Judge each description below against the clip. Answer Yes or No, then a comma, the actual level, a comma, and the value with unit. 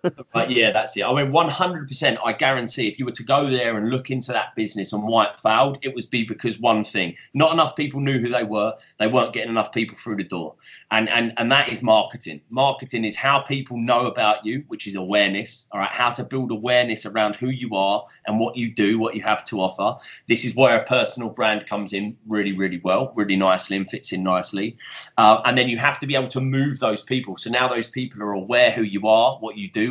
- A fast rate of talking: Yes, fast, 245 wpm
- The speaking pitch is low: Yes, low, 115 Hz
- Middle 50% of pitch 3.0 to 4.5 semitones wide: Yes, average, 3.4 semitones